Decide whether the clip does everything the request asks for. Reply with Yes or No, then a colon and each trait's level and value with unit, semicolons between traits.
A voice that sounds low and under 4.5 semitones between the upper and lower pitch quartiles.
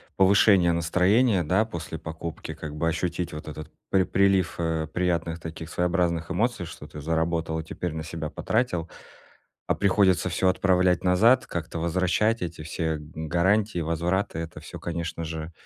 Yes: very low, 85 Hz; narrow, 2.4 semitones